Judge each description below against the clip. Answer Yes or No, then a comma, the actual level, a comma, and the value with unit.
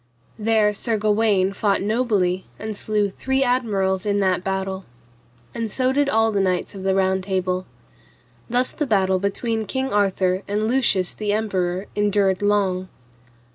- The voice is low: No, high, 205 Hz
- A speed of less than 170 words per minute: Yes, average, 150 wpm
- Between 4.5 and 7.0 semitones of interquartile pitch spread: No, average, 2.7 semitones